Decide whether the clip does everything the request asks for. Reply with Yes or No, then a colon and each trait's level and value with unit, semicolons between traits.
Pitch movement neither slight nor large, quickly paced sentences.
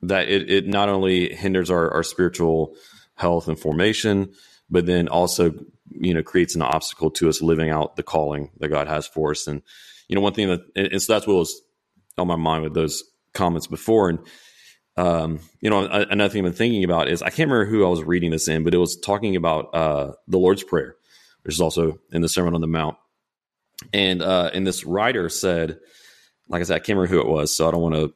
Yes: average, 3.2 semitones; fast, 230 wpm